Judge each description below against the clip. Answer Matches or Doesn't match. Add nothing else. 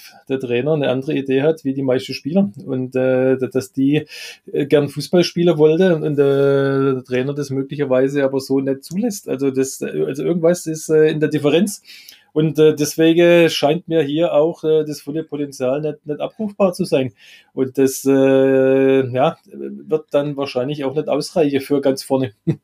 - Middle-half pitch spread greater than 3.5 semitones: Doesn't match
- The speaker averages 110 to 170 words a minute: Doesn't match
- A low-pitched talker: Doesn't match